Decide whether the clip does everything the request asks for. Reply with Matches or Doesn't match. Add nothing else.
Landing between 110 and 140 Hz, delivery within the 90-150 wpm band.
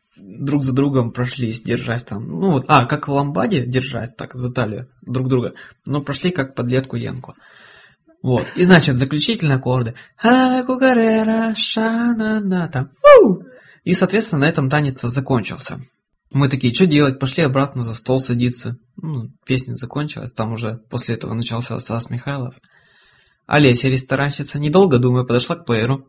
Matches